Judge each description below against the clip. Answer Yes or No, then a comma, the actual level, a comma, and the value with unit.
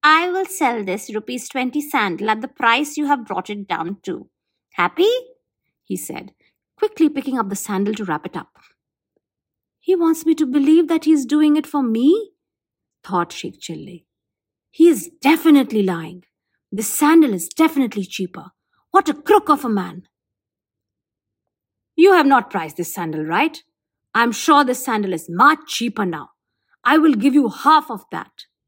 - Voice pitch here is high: Yes, very high, 250 Hz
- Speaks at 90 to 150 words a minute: No, average, 170 wpm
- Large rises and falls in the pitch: Yes, wide, 8.8 semitones